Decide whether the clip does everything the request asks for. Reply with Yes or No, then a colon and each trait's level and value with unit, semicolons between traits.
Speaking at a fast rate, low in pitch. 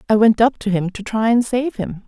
No: fast, 290 wpm; high, 220 Hz